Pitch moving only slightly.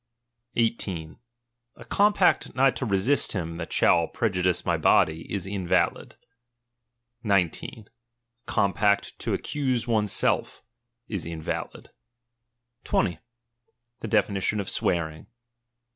No: average, 5.1 semitones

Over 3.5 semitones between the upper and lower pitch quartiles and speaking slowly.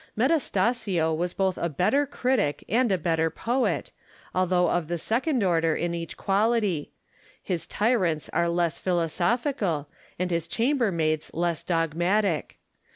Yes: average, 5.3 semitones; slow, 130 wpm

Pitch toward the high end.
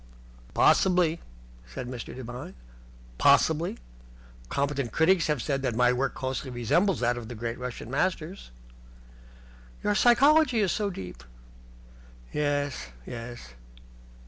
No: low, 135 Hz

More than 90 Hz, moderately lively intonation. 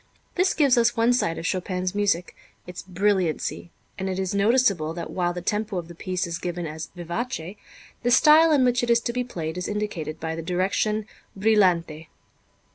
Yes: high, 190 Hz; average, 4.9 semitones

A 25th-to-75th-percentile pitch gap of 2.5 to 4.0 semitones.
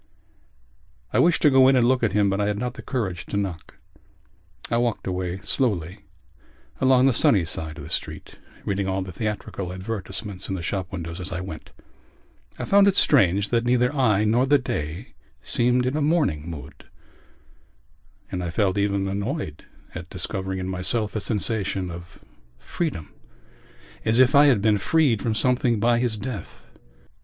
No: average, 5.0 semitones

